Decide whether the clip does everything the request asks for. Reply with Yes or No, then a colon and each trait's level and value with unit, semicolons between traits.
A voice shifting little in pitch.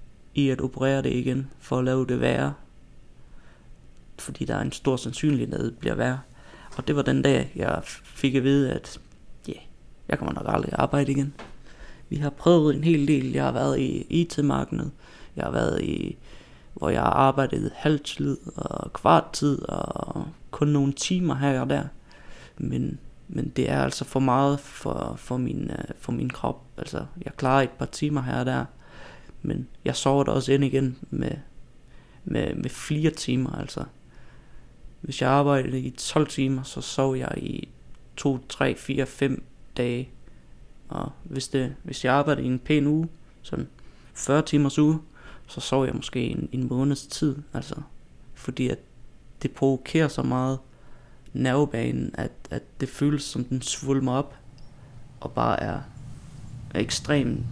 Yes: narrow, 2.2 semitones